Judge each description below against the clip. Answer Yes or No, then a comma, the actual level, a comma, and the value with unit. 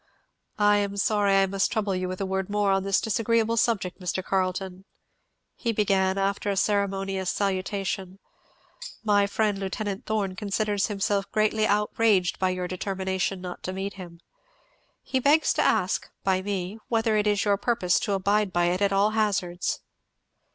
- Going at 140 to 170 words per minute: Yes, average, 165 wpm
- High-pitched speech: Yes, high, 195 Hz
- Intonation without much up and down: Yes, narrow, 1.8 semitones